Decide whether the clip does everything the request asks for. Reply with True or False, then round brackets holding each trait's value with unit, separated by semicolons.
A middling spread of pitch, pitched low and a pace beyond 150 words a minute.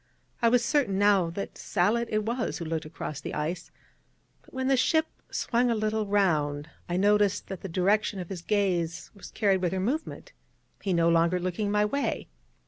False (3.9 semitones; 200 Hz; 190 wpm)